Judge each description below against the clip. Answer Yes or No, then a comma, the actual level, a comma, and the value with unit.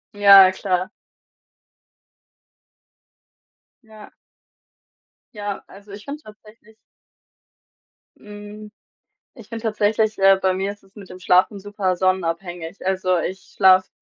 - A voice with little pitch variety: Yes, narrow, 2.2 semitones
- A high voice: Yes, high, 200 Hz